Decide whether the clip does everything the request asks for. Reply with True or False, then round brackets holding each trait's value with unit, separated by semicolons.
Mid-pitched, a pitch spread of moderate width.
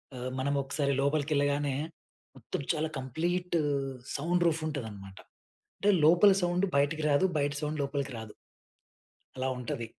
True (145 Hz; 3.0 semitones)